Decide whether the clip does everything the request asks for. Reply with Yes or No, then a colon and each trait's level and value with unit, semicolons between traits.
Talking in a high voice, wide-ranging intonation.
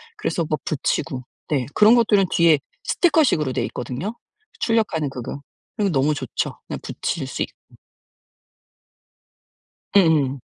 No: medium, 160 Hz; wide, 7.4 semitones